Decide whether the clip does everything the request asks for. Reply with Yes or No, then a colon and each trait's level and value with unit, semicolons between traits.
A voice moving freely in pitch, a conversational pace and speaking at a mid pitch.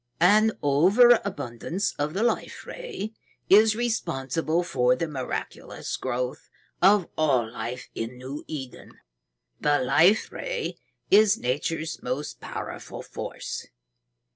No: wide, 8.4 semitones; slow, 110 wpm; medium, 155 Hz